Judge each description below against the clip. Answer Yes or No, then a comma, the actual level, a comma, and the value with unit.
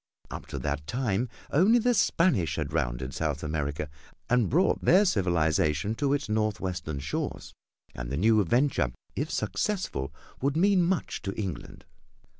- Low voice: Yes, low, 105 Hz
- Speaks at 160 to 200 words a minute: No, average, 145 wpm